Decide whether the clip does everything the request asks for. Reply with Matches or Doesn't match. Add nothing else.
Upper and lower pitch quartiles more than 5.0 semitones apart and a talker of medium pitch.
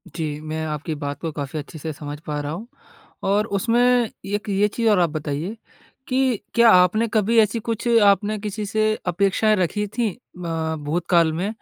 Doesn't match